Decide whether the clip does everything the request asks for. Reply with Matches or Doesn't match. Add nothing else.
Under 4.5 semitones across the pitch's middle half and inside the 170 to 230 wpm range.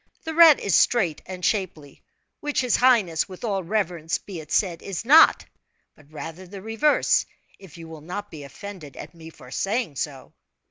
Doesn't match